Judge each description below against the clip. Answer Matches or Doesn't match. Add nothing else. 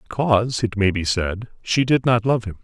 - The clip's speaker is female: Doesn't match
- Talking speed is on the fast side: Matches